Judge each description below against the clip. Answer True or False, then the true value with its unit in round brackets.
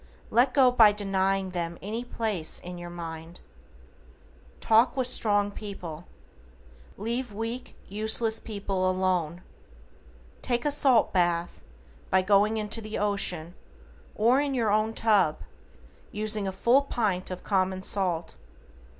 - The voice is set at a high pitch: True (205 Hz)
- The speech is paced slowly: True (125 wpm)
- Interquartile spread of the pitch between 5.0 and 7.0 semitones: False (3.5 semitones)